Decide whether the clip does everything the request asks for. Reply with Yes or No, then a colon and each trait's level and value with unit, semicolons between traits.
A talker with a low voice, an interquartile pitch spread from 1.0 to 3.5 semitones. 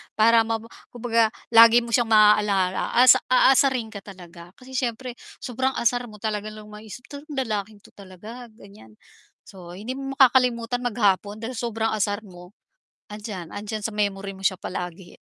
No: high, 215 Hz; average, 3.2 semitones